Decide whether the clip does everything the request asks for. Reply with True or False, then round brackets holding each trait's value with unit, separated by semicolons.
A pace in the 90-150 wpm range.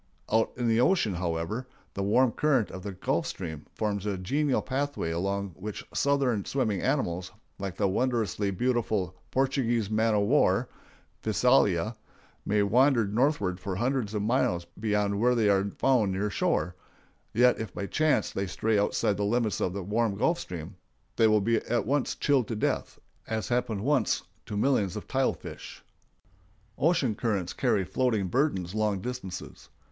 False (160 wpm)